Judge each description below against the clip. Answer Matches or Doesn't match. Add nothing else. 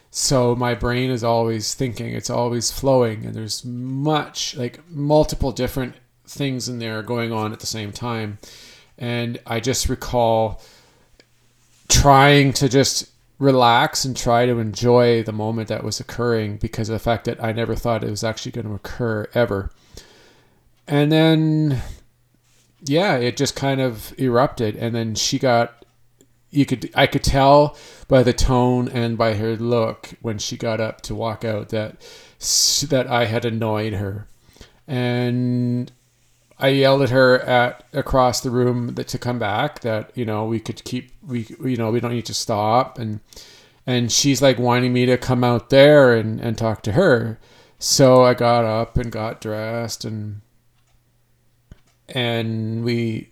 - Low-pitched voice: Matches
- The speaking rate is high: Doesn't match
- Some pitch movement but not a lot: Doesn't match